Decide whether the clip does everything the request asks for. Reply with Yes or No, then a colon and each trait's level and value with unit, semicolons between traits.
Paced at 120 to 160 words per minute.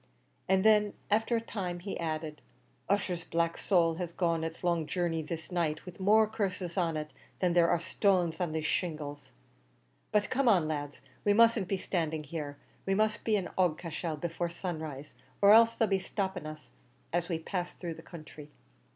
No: average, 180 wpm